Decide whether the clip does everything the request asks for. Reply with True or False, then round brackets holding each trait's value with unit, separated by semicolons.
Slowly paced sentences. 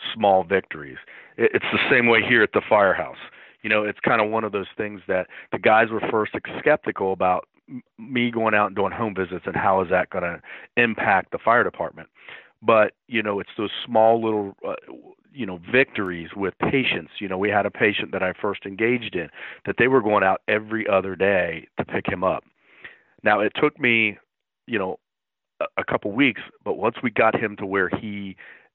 False (200 wpm)